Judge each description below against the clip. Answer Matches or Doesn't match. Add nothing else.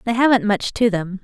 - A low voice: Doesn't match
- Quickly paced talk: Matches